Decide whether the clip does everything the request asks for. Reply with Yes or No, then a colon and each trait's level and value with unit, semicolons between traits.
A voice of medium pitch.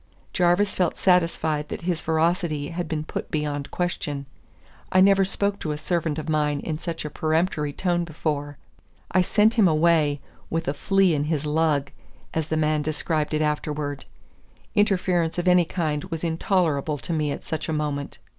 Yes: medium, 160 Hz